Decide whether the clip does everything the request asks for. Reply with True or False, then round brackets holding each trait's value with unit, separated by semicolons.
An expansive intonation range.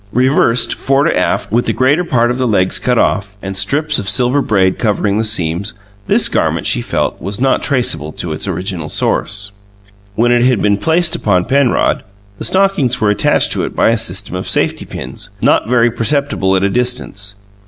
False (4.7 semitones)